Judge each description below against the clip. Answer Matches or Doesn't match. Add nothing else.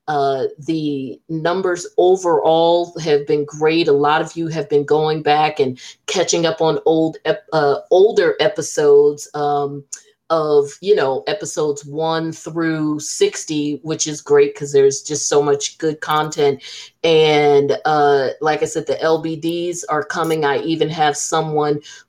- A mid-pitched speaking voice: Matches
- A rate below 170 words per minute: Matches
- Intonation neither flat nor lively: Doesn't match